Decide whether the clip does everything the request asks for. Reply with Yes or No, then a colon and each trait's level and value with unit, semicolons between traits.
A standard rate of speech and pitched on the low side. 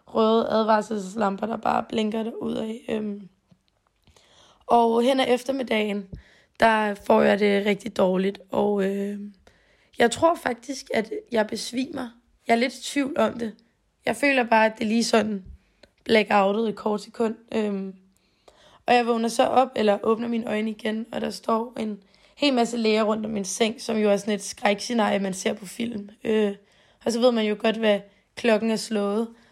No: average, 175 wpm; high, 220 Hz